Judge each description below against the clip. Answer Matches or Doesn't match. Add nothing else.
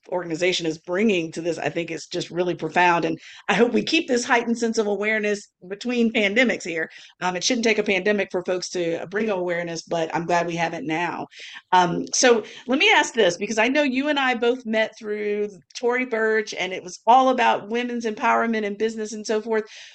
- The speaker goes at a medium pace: Doesn't match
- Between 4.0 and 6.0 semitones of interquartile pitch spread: Matches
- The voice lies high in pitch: Matches